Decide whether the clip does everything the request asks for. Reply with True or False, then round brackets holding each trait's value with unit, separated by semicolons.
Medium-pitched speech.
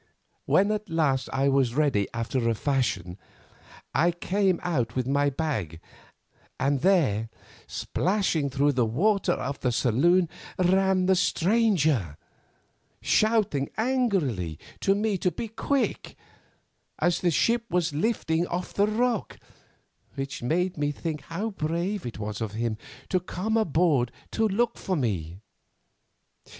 True (160 Hz)